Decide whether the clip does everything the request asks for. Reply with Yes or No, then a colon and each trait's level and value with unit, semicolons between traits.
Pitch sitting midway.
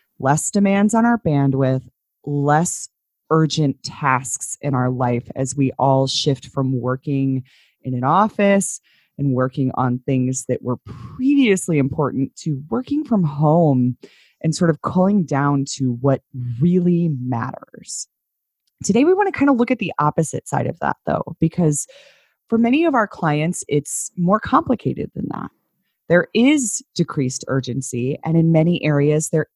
Yes: medium, 150 Hz